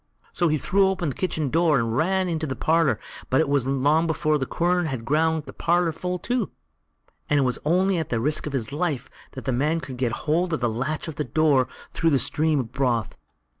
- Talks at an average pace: No, fast, 235 wpm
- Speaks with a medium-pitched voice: Yes, medium, 155 Hz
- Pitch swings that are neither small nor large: Yes, average, 4.0 semitones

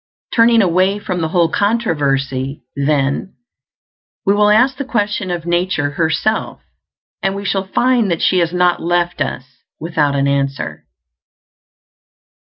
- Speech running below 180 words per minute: Yes, slow, 135 wpm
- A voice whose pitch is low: No, medium, 175 Hz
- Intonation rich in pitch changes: Yes, wide, 6.0 semitones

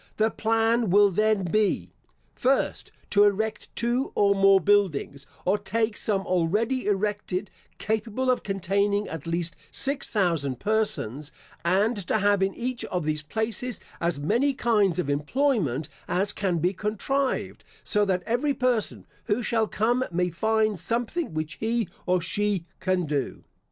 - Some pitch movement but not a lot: Yes, average, 3.8 semitones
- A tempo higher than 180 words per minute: No, average, 145 wpm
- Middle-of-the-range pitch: No, high, 205 Hz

